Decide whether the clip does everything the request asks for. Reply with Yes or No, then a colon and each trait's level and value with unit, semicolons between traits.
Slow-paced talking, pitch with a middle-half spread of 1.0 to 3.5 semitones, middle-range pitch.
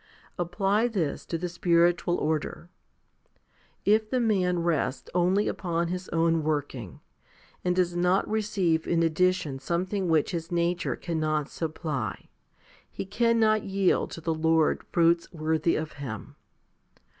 Yes: slow, 130 wpm; narrow, 2.6 semitones; medium, 170 Hz